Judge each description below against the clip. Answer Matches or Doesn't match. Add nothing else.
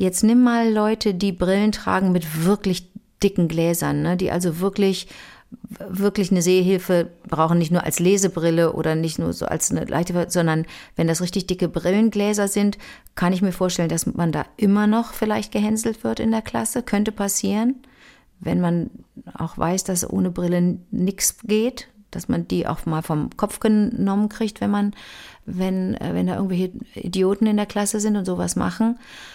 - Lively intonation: Doesn't match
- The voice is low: Doesn't match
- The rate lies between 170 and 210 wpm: Matches